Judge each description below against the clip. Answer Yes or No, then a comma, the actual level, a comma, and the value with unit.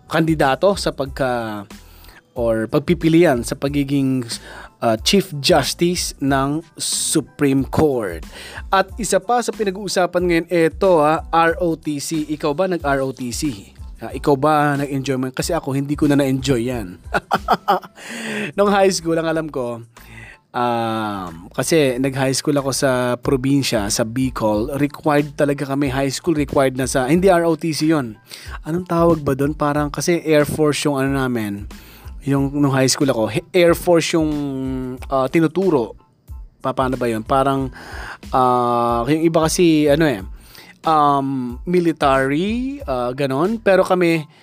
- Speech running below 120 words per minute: No, average, 140 wpm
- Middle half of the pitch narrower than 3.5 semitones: No, average, 4.0 semitones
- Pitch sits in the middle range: Yes, medium, 145 Hz